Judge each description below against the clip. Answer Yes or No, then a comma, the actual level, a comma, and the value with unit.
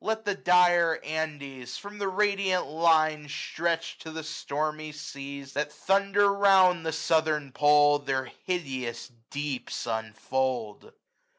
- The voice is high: No, medium, 155 Hz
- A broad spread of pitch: No, average, 4.3 semitones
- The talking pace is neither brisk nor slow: No, slow, 120 wpm